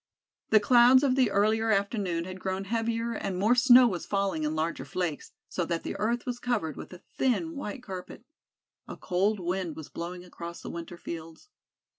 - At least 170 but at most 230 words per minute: Yes, average, 185 wpm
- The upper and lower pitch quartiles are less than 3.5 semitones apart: No, average, 5.2 semitones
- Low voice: No, high, 195 Hz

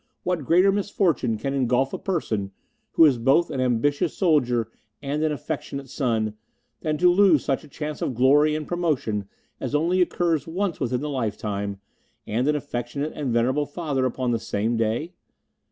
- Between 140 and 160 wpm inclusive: No, average, 170 wpm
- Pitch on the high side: No, medium, 140 Hz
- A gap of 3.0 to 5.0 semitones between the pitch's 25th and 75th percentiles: Yes, average, 4.7 semitones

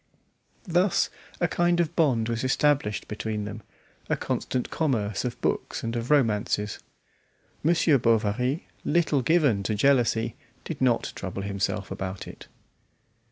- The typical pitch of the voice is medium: No, low, 120 Hz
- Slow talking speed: Yes, slow, 130 wpm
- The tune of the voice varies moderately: No, wide, 6.0 semitones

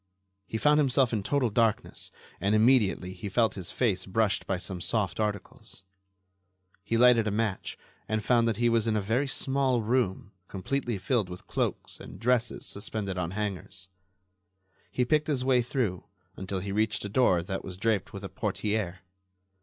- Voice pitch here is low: Yes, low, 110 Hz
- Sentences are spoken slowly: No, average, 170 wpm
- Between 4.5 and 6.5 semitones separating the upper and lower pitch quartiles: No, average, 4.0 semitones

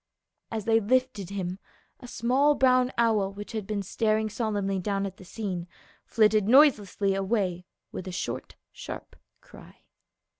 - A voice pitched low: No, high, 210 Hz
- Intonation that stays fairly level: No, average, 3.2 semitones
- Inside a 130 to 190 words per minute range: Yes, average, 150 wpm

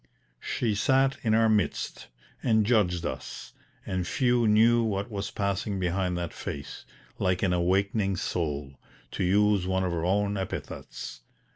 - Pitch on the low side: Yes, low, 100 Hz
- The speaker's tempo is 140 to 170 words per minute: Yes, average, 145 wpm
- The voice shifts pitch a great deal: No, average, 3.4 semitones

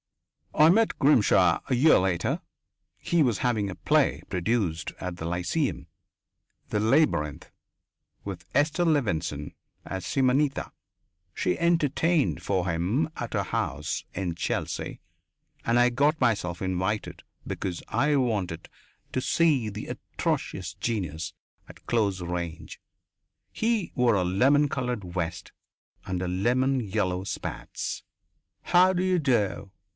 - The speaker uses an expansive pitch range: Yes, wide, 7.5 semitones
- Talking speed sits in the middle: No, slow, 120 wpm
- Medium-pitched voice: No, low, 110 Hz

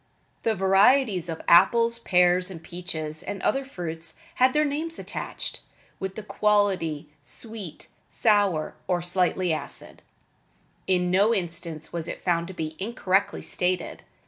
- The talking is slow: Yes, slow, 130 wpm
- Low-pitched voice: No, medium, 185 Hz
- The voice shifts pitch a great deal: No, average, 3.8 semitones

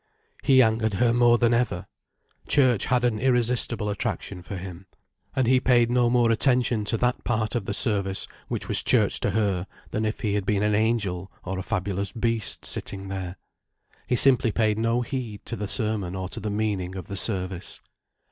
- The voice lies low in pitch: Yes, low, 110 Hz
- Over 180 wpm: Yes, average, 190 wpm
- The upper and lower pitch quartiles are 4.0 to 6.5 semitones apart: No, average, 3.5 semitones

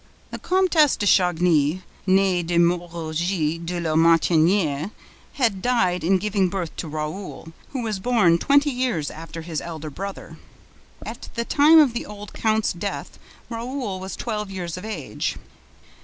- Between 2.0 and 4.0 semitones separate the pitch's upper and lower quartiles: No, average, 4.8 semitones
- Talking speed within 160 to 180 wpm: No, average, 150 wpm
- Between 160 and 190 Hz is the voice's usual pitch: Yes, medium, 185 Hz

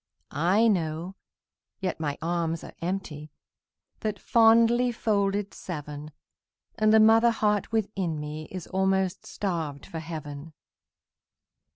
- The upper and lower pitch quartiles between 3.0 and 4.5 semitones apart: No, average, 5.2 semitones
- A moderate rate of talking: No, slow, 110 wpm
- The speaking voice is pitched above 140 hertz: Yes, medium, 185 Hz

